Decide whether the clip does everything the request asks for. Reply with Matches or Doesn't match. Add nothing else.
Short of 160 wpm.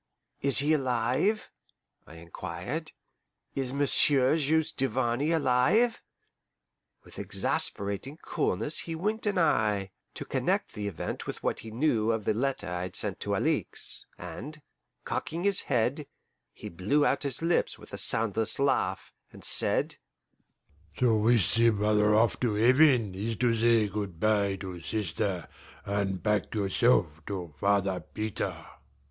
Matches